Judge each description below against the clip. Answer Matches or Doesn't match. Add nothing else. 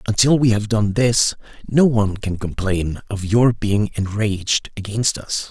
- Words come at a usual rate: Matches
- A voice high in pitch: Doesn't match